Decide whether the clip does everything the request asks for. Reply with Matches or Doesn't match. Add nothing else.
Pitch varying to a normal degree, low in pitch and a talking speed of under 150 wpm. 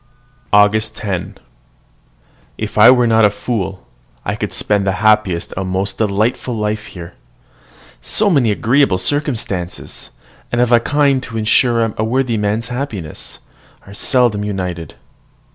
Matches